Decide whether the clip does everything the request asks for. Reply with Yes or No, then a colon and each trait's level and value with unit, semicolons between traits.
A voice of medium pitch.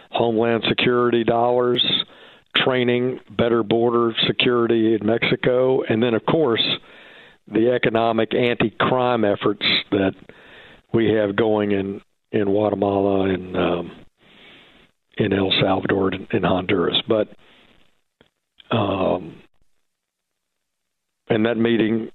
No: low, 115 Hz